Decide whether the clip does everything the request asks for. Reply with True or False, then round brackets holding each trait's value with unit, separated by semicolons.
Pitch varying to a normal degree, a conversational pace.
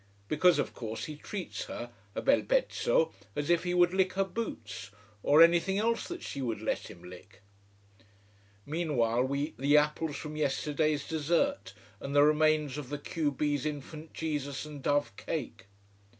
True (3.6 semitones; 165 wpm)